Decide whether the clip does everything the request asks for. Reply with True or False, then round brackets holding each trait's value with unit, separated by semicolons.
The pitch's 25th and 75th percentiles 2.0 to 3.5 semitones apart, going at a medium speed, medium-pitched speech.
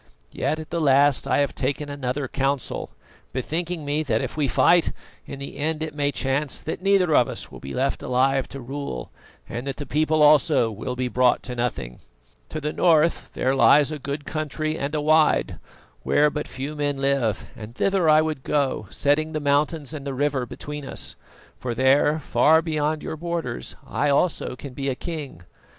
True (2.7 semitones; 190 wpm; 145 Hz)